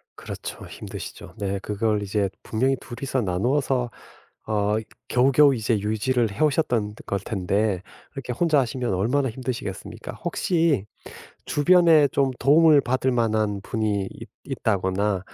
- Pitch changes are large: No, average, 4.8 semitones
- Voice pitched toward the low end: Yes, low, 115 Hz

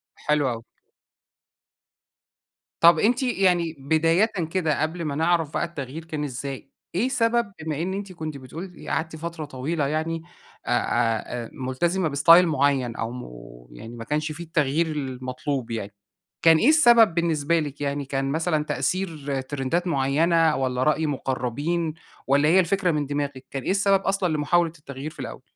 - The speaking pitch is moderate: Yes, medium, 155 Hz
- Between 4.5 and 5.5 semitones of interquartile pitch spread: No, average, 3.8 semitones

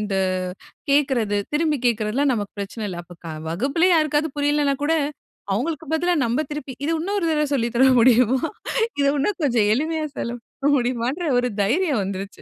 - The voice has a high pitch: Yes, very high, 265 Hz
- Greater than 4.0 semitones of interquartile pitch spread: Yes, average, 5.1 semitones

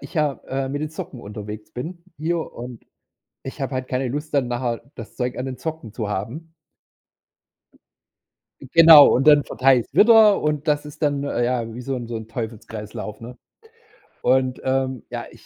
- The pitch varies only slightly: No, average, 3.9 semitones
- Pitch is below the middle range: Yes, low, 130 Hz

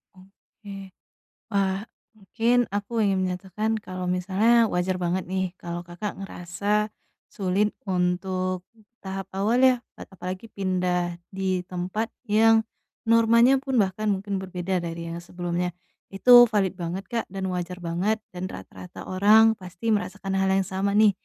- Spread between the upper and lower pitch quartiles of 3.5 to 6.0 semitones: No, average, 2.7 semitones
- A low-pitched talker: No, high, 190 Hz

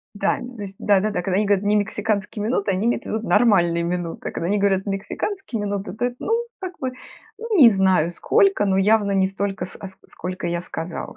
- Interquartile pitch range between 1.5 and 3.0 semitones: Yes, average, 2.7 semitones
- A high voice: Yes, high, 200 Hz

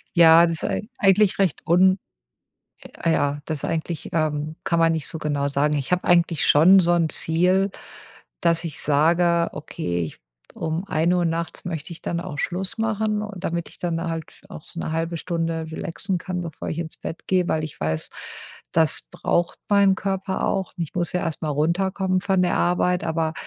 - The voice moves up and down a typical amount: No, narrow, 2.3 semitones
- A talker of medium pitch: Yes, medium, 170 Hz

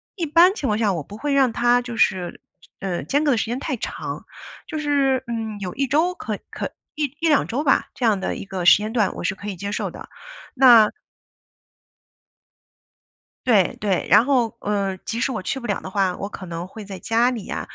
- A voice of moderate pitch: No, high, 225 Hz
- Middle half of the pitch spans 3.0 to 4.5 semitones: No, average, 5.3 semitones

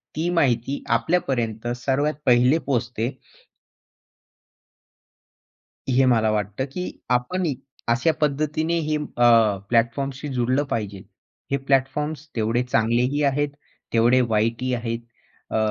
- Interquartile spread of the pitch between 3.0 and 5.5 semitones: Yes, average, 3.9 semitones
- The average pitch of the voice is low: Yes, low, 125 Hz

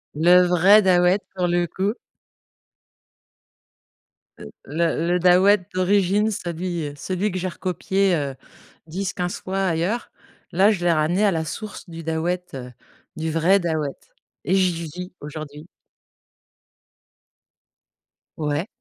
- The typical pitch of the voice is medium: Yes, medium, 180 Hz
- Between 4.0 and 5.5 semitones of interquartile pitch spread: No, average, 2.7 semitones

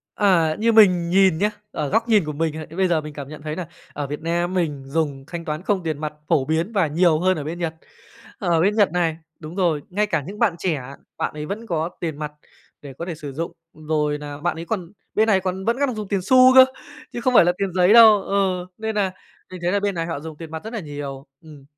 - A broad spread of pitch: No, average, 4.3 semitones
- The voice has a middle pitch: Yes, medium, 170 Hz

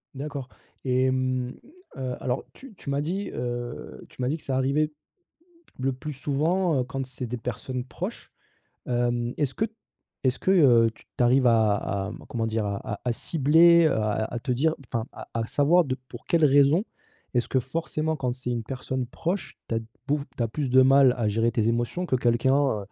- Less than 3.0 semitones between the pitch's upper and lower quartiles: No, average, 3.3 semitones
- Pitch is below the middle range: Yes, low, 130 Hz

